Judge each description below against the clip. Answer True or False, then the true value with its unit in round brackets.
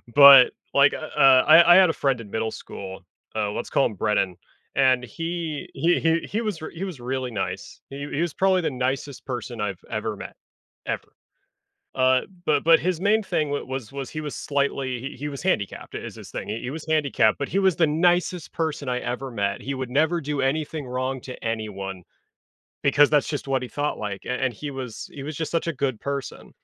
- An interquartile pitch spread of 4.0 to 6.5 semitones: True (4.3 semitones)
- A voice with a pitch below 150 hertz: True (135 Hz)